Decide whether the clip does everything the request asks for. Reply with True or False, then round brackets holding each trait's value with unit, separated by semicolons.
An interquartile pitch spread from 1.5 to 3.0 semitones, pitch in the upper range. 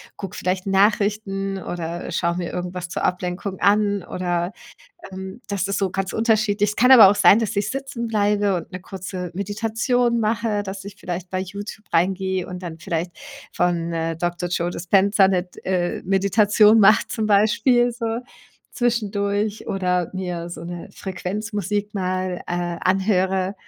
True (2.7 semitones; 195 Hz)